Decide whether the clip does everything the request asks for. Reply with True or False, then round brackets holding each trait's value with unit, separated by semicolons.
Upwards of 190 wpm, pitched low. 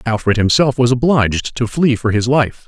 True (200 wpm; 120 Hz)